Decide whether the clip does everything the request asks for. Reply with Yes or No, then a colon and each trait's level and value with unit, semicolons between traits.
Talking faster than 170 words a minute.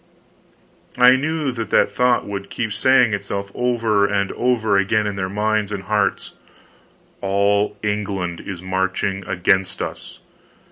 No: slow, 135 wpm